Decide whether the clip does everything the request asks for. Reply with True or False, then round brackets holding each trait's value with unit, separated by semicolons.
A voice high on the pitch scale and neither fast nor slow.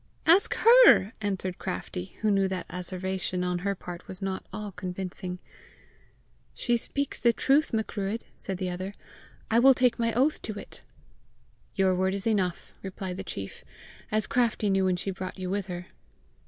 True (195 Hz; 170 wpm)